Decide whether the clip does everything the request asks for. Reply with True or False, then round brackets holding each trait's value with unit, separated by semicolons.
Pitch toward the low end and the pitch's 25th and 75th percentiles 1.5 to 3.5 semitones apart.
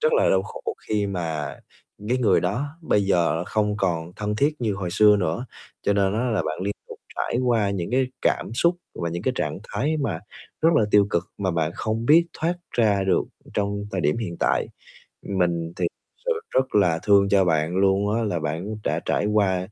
False (100 Hz; 4.2 semitones)